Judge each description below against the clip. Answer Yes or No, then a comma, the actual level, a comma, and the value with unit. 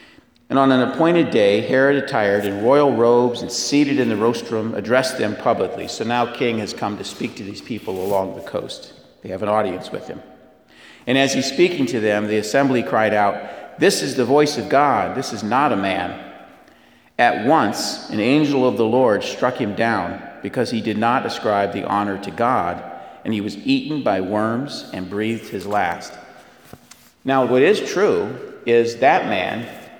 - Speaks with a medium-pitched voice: No, low, 115 Hz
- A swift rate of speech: No, average, 190 wpm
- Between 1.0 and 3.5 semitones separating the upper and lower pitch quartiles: No, average, 4.1 semitones